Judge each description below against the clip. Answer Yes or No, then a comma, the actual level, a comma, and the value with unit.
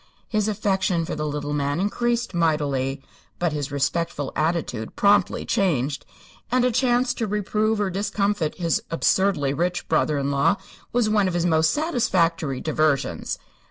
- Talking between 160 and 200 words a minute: No, average, 150 wpm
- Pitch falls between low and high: Yes, medium, 170 Hz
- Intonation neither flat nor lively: No, wide, 5.9 semitones